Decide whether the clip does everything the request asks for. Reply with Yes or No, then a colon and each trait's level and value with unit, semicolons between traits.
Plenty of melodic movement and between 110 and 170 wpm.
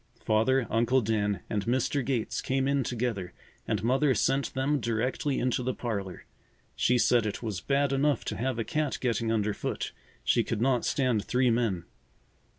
No: average, 3.2 semitones; average, 165 wpm